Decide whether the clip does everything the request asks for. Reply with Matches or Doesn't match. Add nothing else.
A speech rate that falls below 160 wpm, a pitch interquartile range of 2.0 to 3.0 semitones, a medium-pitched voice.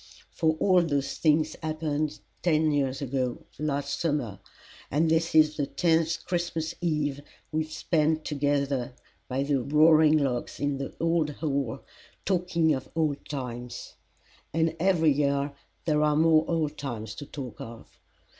Matches